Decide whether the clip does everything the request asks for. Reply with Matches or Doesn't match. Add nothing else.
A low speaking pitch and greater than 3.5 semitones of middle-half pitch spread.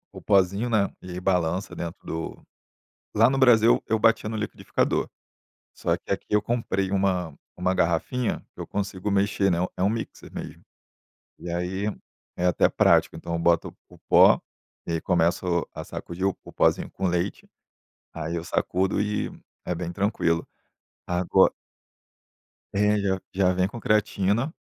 Doesn't match